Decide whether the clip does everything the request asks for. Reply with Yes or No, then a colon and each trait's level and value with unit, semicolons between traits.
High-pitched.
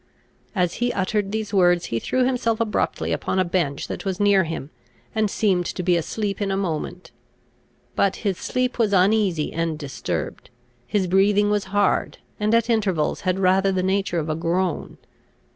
Yes: high, 195 Hz